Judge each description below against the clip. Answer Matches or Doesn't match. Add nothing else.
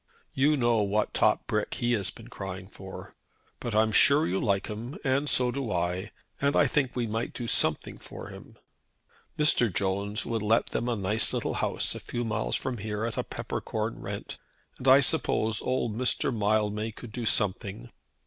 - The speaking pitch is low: Matches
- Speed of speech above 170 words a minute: Matches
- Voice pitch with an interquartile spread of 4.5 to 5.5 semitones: Doesn't match